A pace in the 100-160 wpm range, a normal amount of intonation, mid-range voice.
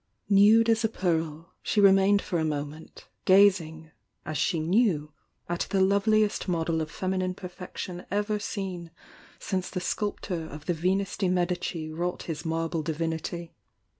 Yes: average, 145 wpm; average, 3.4 semitones; medium, 180 Hz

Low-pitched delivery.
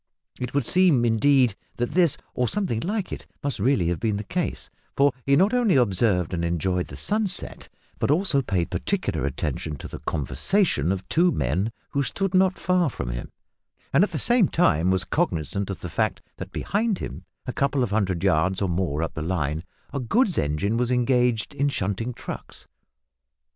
Yes: low, 115 Hz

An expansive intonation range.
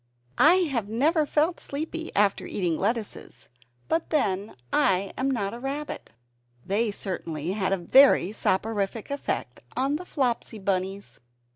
Yes: wide, 6.4 semitones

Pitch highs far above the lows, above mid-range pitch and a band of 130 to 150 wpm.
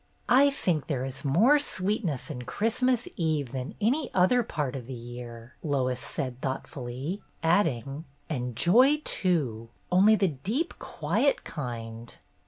No: wide, 8.5 semitones; medium, 150 Hz; average, 140 wpm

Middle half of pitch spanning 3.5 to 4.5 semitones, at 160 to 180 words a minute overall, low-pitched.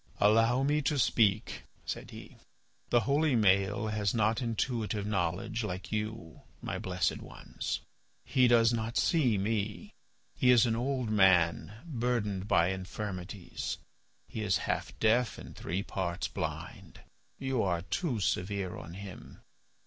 No: average, 4.0 semitones; slow, 135 wpm; low, 105 Hz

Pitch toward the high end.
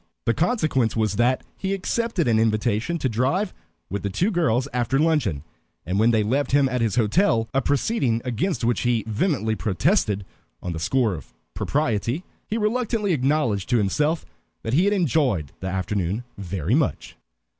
No: low, 125 Hz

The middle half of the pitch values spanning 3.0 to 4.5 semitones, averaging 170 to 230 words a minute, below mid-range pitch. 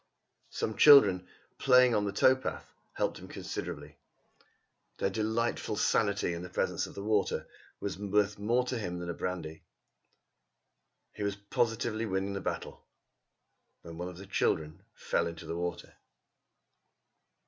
No: average, 3.8 semitones; average, 145 wpm; low, 100 Hz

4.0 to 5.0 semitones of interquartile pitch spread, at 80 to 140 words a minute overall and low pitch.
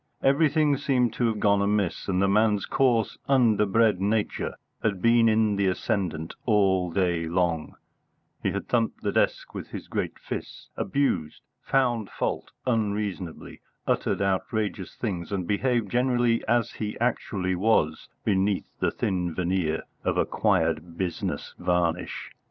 Yes: average, 4.3 semitones; slow, 135 wpm; low, 105 Hz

